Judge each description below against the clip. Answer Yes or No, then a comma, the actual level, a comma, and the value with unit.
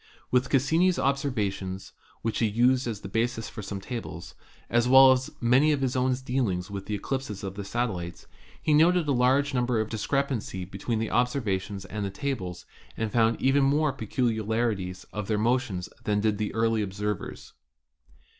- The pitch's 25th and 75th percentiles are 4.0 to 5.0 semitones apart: Yes, average, 4.4 semitones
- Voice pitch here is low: Yes, low, 115 Hz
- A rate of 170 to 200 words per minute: Yes, average, 175 wpm